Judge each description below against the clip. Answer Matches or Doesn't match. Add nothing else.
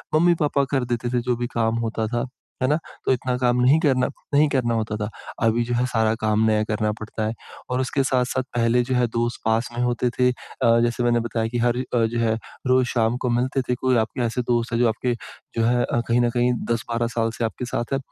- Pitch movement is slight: Matches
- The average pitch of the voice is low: Matches